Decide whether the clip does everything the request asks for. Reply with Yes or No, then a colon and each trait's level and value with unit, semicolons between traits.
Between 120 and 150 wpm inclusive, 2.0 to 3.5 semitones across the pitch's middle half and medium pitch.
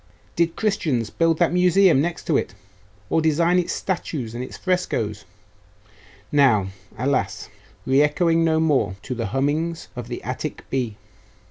No: average, 145 wpm; wide, 5.4 semitones; medium, 150 Hz